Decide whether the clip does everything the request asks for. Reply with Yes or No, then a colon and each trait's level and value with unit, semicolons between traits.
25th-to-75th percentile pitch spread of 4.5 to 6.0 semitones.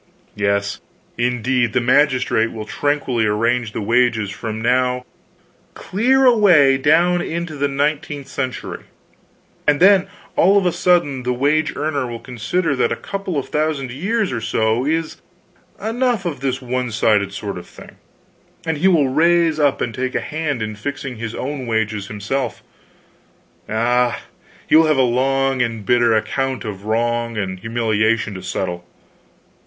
Yes: average, 5.1 semitones